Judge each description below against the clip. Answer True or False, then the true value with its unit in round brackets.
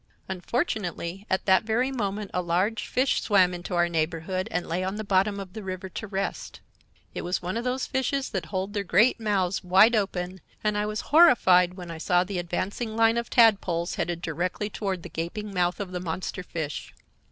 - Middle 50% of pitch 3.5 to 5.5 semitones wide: False (3.1 semitones)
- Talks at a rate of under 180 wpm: False (200 wpm)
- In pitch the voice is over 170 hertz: True (190 Hz)